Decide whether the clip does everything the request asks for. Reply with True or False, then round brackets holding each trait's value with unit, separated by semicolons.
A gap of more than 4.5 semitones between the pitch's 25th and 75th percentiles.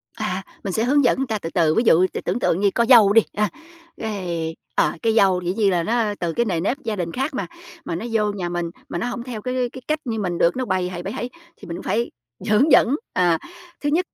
True (5.1 semitones)